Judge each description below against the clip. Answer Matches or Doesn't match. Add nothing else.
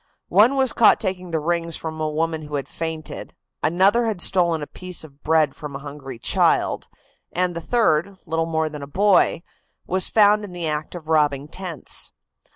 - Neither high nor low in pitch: Matches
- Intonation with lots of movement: Doesn't match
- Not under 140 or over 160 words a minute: Doesn't match